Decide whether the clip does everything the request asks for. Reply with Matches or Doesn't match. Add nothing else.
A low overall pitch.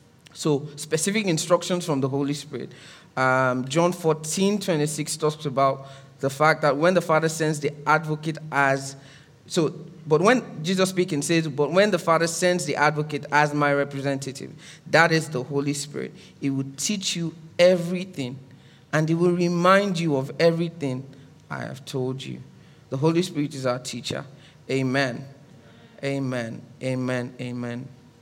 Doesn't match